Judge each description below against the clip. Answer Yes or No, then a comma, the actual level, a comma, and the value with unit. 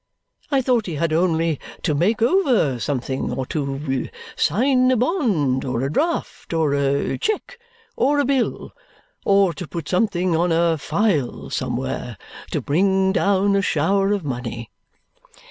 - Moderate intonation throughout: No, wide, 7.5 semitones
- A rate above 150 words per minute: No, average, 145 wpm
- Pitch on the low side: No, medium, 175 Hz